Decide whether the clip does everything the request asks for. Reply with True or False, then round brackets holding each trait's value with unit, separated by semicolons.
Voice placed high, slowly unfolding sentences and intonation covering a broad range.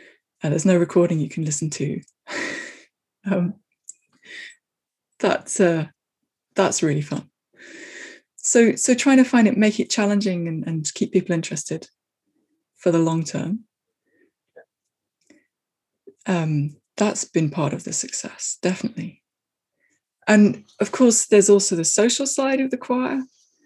True (205 Hz; 130 wpm; 7.0 semitones)